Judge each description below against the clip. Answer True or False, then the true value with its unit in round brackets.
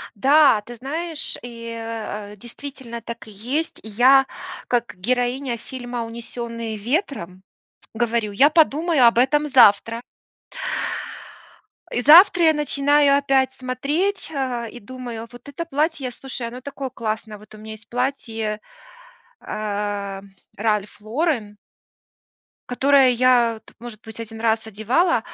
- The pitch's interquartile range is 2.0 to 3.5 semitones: False (3.9 semitones)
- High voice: True (240 Hz)